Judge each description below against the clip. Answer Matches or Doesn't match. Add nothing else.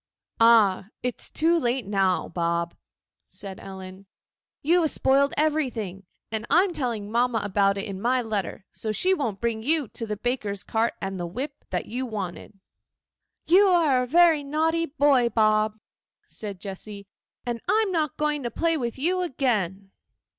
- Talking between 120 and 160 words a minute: Doesn't match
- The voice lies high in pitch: Matches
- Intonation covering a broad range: Matches